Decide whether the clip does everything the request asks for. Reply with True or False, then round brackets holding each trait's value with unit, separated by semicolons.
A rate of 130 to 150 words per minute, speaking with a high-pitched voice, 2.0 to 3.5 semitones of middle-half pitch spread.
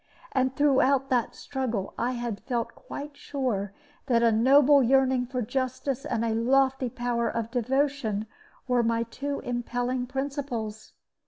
True (140 wpm; 250 Hz; 2.6 semitones)